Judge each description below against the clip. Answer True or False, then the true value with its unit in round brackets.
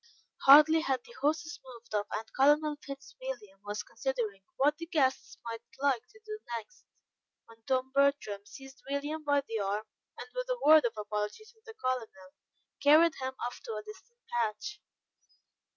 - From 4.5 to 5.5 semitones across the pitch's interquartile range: True (5.2 semitones)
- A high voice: True (270 Hz)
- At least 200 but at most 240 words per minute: False (165 wpm)